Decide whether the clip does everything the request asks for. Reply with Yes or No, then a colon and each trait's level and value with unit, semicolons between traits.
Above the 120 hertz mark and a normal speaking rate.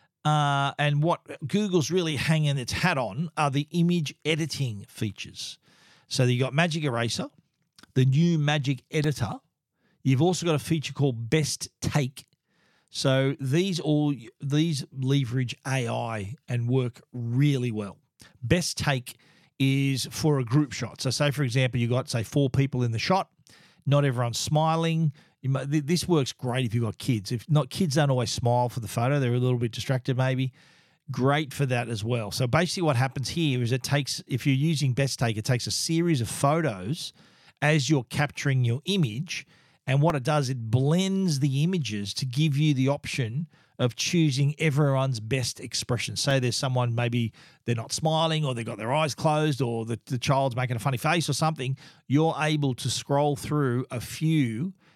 Yes: medium, 140 Hz; average, 180 wpm